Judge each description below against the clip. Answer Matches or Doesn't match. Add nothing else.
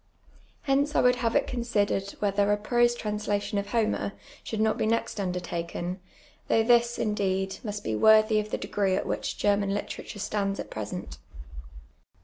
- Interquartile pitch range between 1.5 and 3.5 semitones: Matches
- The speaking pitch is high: Matches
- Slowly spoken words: Doesn't match